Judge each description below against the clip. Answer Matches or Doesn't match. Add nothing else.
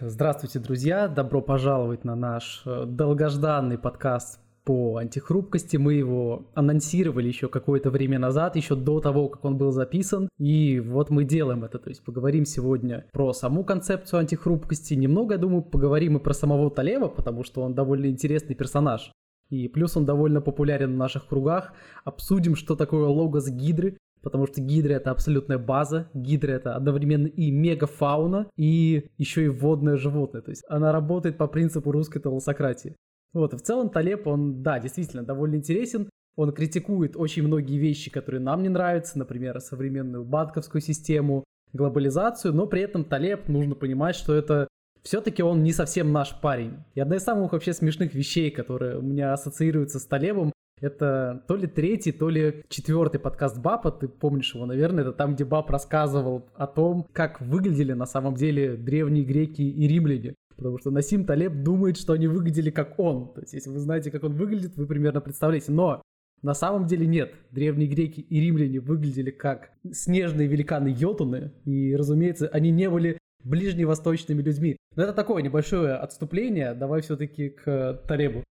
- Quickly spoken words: Matches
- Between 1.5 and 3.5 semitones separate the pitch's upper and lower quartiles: Matches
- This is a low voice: Doesn't match